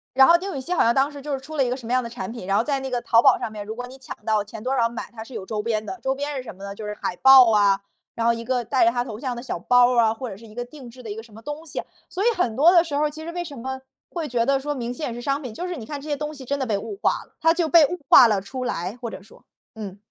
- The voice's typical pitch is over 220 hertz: Yes, very high, 250 Hz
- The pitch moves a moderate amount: Yes, average, 4.1 semitones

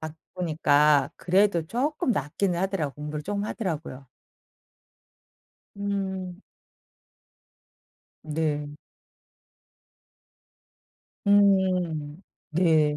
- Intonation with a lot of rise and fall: No, average, 4.5 semitones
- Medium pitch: Yes, medium, 170 Hz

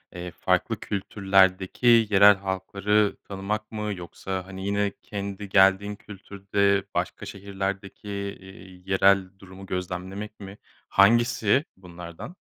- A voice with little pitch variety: Yes, narrow, 1.4 semitones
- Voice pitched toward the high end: No, low, 100 Hz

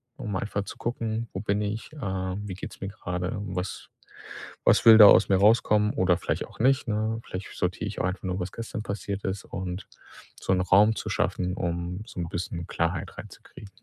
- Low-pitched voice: Yes, low, 100 Hz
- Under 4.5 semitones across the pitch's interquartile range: Yes, narrow, 2.6 semitones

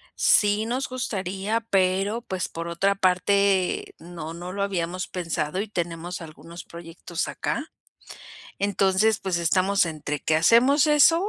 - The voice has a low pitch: No, medium, 185 Hz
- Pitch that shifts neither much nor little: Yes, average, 3.2 semitones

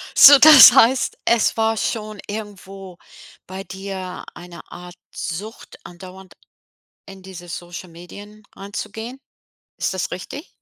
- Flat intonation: No, average, 3.5 semitones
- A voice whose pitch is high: Yes, high, 195 Hz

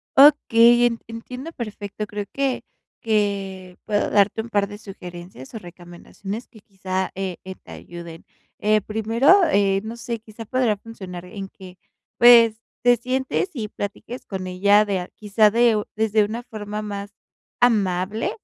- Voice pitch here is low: No, high, 210 Hz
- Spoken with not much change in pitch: No, average, 3.0 semitones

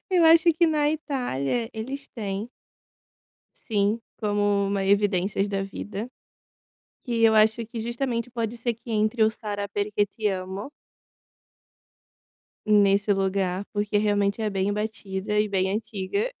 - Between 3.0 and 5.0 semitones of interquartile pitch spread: No, narrow, 2.6 semitones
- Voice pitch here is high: Yes, high, 210 Hz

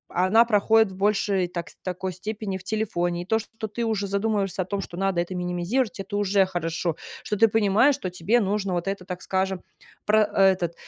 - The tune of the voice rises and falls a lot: No, average, 2.8 semitones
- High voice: Yes, high, 195 Hz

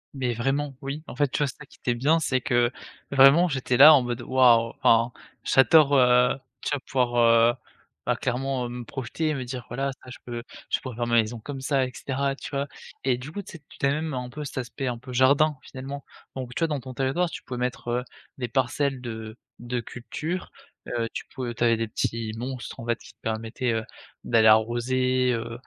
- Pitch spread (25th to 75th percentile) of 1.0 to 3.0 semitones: Yes, narrow, 2.4 semitones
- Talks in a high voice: No, low, 130 Hz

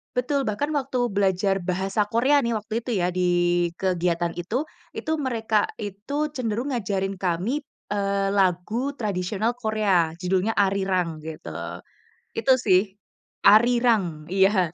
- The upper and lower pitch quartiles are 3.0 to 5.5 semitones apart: Yes, average, 3.5 semitones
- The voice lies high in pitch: Yes, high, 200 Hz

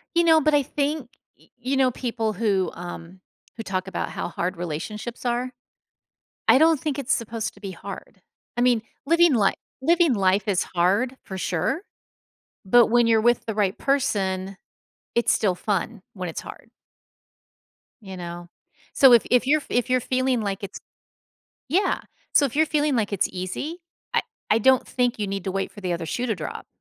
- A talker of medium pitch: No, high, 225 Hz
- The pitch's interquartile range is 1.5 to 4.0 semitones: No, wide, 5.4 semitones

